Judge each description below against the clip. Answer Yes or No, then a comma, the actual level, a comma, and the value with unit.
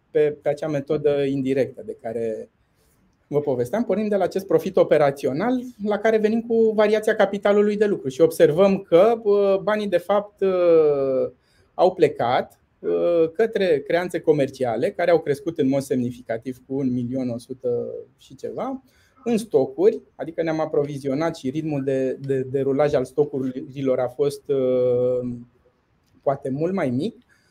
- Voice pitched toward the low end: No, medium, 150 Hz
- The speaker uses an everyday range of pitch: No, wide, 7.5 semitones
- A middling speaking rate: Yes, average, 135 wpm